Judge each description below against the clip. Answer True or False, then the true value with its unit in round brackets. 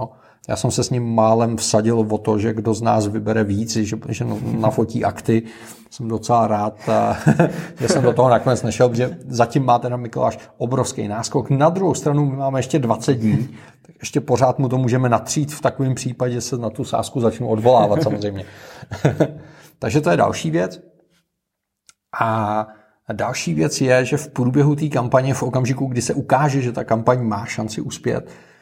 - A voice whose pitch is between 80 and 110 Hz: False (120 Hz)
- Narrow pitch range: False (3.2 semitones)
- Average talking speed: False (180 wpm)